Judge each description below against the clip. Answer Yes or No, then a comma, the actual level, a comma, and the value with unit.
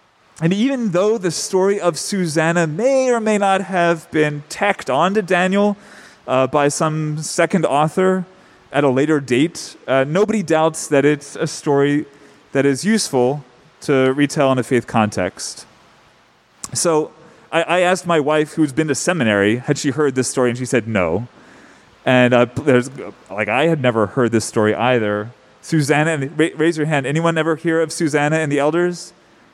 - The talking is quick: No, average, 170 wpm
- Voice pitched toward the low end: No, medium, 150 Hz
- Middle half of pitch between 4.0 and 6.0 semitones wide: Yes, average, 4.7 semitones